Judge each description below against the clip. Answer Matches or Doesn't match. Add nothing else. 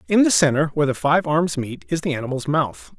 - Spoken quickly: Matches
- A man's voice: Matches